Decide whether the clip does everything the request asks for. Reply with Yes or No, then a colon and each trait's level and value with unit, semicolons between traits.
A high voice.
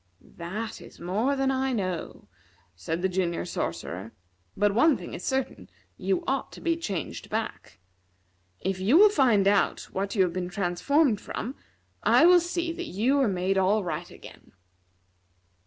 Yes: high, 200 Hz